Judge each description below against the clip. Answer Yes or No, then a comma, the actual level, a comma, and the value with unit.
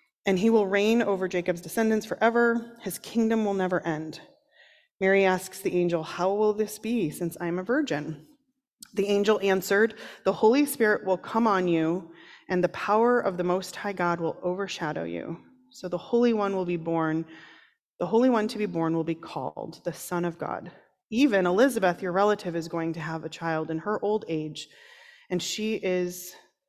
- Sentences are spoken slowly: No, average, 190 wpm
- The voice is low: No, high, 190 Hz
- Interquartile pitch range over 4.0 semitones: Yes, average, 4.5 semitones